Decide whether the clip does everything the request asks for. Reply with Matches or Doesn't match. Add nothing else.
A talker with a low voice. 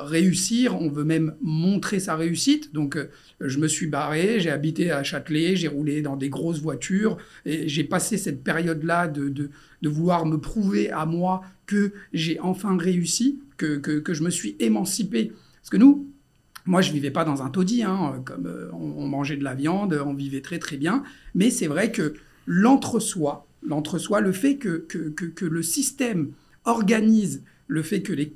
Doesn't match